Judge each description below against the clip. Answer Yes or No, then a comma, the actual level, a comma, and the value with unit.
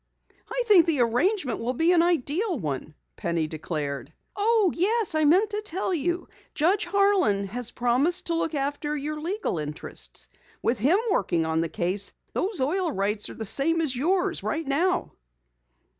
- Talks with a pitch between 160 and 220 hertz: No, very high, 305 Hz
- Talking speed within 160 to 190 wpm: Yes, average, 165 wpm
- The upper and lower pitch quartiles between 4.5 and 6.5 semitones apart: No, wide, 8.7 semitones